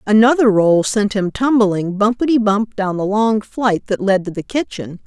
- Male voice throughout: No, female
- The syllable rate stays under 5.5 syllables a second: Yes, 4.5 syllables/s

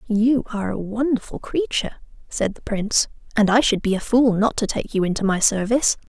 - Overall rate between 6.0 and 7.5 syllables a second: No, 5.7 syllables/s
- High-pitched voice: Yes, high, 220 Hz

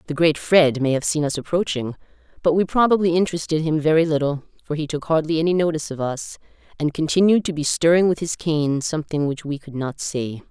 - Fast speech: Yes, fast, 210 wpm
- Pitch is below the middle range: No, medium, 155 Hz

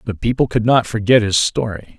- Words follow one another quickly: Yes, fast, 210 wpm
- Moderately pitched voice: No, low, 110 Hz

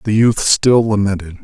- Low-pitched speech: Yes, low, 105 Hz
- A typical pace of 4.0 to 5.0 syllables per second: Yes, 4.6 syllables/s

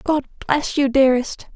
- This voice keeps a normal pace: Yes, average, 155 wpm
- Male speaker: No, female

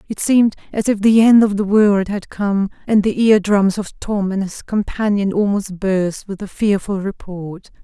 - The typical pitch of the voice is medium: No, high, 200 Hz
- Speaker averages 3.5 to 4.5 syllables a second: Yes, 4.4 syllables/s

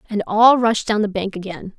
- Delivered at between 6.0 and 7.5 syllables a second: No, 5.0 syllables/s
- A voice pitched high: Yes, high, 210 Hz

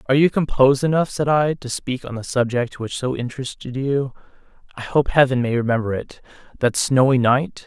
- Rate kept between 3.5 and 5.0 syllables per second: No, 5.5 syllables/s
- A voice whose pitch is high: No, low, 130 Hz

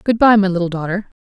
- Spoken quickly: Yes, fast, 245 wpm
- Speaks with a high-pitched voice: Yes, high, 195 Hz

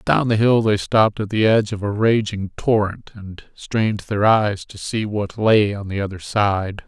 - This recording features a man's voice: Yes, male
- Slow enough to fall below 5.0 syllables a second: Yes, 4.5 syllables/s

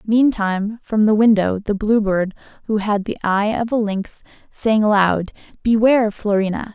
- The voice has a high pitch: Yes, high, 210 Hz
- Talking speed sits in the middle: Yes, average, 160 wpm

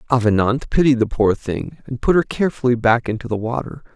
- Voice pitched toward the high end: No, low, 120 Hz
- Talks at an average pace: Yes, average, 195 wpm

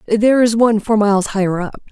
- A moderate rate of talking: No, fast, 220 wpm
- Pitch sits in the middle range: No, high, 215 Hz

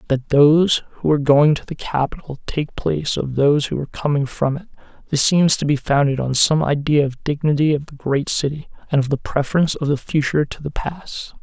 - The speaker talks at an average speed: No, fast, 215 wpm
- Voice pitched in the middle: Yes, medium, 145 Hz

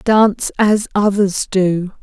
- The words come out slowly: Yes, slow, 120 wpm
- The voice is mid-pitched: No, high, 200 Hz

